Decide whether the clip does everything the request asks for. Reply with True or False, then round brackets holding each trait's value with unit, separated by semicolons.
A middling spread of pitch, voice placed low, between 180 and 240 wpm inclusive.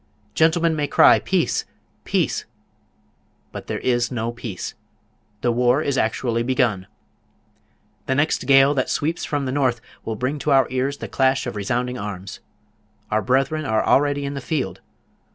False (3.2 semitones; 130 Hz; 155 wpm)